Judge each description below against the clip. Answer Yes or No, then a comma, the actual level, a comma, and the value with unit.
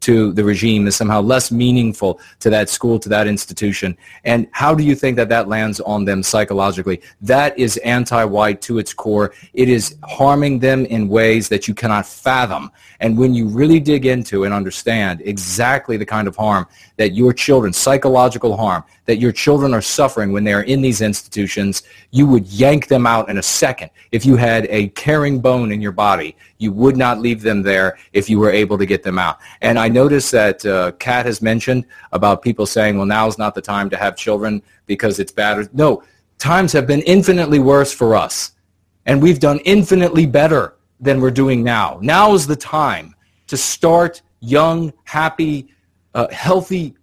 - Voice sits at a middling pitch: No, low, 115 Hz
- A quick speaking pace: No, average, 190 wpm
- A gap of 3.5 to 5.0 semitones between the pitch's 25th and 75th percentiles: Yes, average, 4.6 semitones